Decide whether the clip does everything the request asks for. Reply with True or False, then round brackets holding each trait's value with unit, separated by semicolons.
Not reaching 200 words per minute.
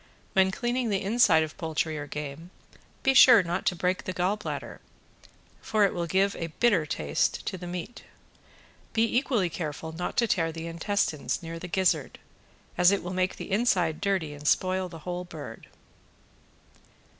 True (170 wpm)